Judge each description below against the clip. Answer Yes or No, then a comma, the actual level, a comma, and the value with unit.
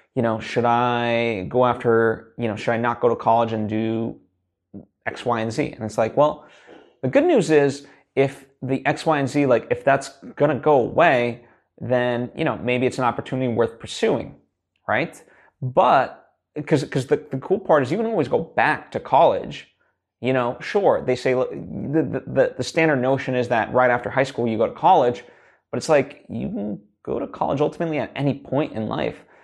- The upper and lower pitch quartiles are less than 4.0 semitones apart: Yes, average, 3.1 semitones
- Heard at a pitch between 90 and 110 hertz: No, low, 125 Hz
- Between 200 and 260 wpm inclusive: Yes, fast, 205 wpm